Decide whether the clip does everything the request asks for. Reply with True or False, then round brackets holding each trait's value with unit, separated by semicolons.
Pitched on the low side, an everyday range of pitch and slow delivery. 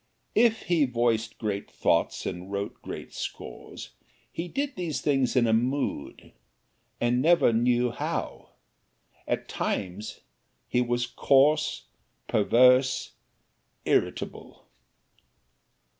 True (125 Hz; 4.2 semitones; 100 wpm)